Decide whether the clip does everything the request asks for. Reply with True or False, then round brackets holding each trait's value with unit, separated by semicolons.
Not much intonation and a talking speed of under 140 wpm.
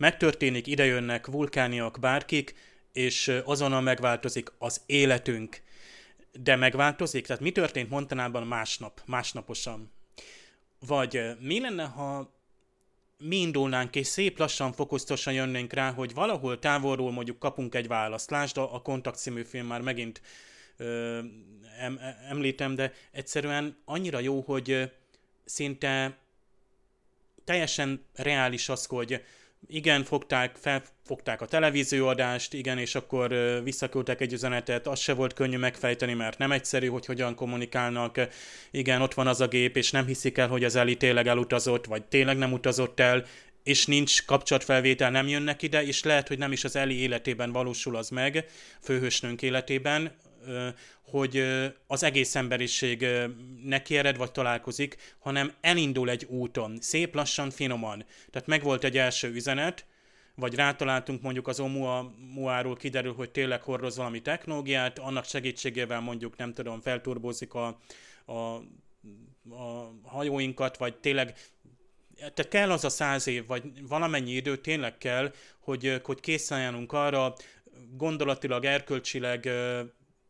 True (2.0 semitones; 130 wpm)